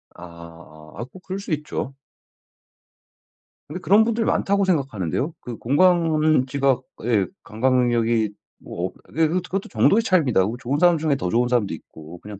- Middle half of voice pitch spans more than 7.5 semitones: Yes, wide, 8.0 semitones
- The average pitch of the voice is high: No, low, 130 Hz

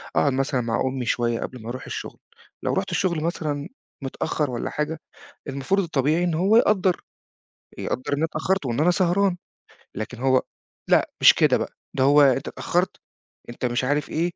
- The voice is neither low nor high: Yes, medium, 145 Hz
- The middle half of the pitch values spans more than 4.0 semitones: Yes, average, 5.0 semitones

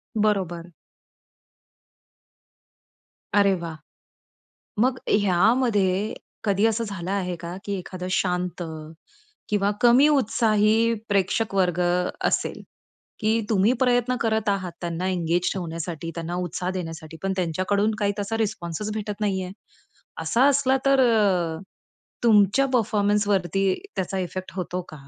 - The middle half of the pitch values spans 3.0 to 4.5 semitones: Yes, average, 3.5 semitones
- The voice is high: Yes, high, 195 Hz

